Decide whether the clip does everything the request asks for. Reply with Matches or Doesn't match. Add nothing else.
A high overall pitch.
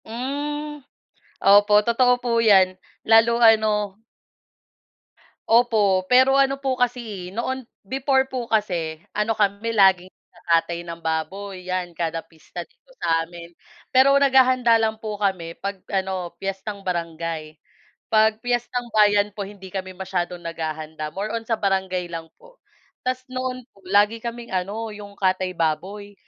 Matches